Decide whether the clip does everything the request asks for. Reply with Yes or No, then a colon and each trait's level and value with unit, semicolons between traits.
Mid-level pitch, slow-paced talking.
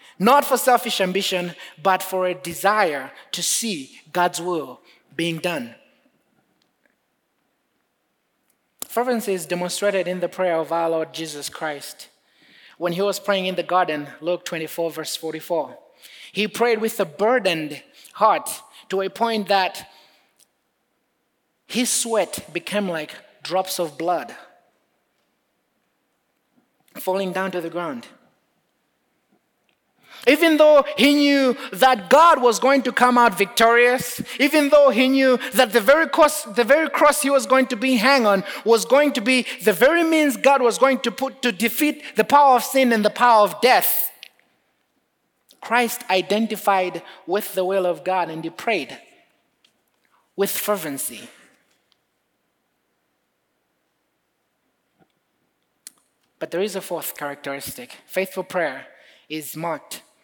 No: high, 205 Hz; slow, 130 wpm